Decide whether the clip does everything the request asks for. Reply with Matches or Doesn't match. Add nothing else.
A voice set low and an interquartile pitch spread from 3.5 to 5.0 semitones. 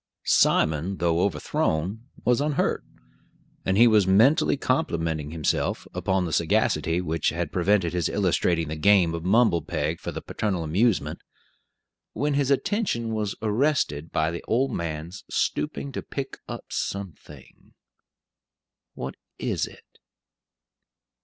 Doesn't match